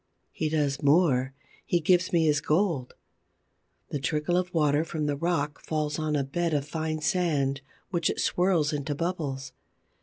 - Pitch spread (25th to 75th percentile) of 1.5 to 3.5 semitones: Yes, average, 3.0 semitones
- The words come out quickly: No, average, 160 wpm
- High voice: No, medium, 155 Hz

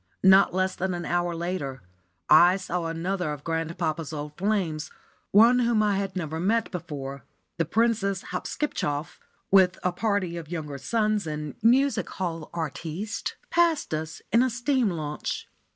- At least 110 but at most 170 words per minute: Yes, average, 150 wpm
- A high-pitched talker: No, medium, 180 Hz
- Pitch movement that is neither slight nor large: Yes, average, 4.5 semitones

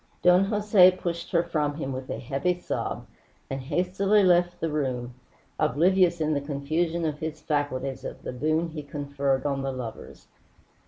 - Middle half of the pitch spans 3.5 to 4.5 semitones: Yes, average, 4.1 semitones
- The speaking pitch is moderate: Yes, medium, 155 Hz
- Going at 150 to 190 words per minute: Yes, average, 165 wpm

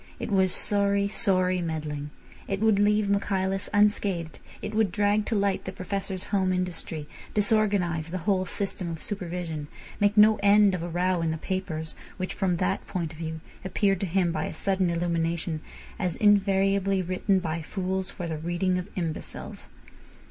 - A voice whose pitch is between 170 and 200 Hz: Yes, medium, 185 Hz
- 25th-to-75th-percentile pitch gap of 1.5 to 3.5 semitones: Yes, average, 2.8 semitones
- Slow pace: No, average, 170 wpm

